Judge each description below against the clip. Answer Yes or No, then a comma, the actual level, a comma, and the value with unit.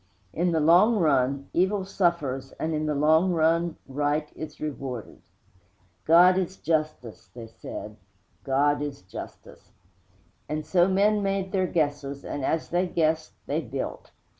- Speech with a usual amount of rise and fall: Yes, average, 3.7 semitones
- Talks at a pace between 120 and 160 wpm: Yes, average, 140 wpm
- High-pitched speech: No, medium, 155 Hz